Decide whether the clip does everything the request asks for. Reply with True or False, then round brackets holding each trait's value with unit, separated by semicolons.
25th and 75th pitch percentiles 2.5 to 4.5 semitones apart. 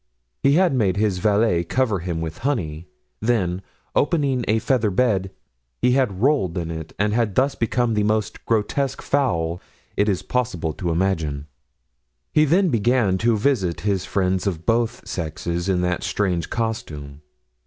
False (5.6 semitones)